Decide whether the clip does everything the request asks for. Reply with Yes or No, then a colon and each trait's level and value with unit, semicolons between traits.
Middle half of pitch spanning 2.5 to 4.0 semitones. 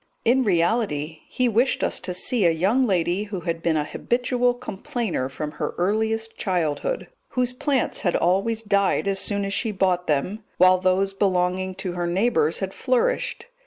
No: average, 4.4 semitones